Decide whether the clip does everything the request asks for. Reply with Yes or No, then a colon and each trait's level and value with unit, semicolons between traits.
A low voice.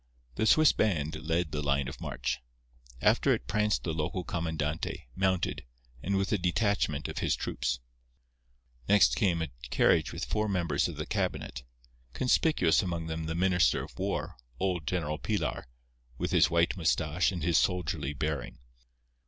Yes: very low, 85 Hz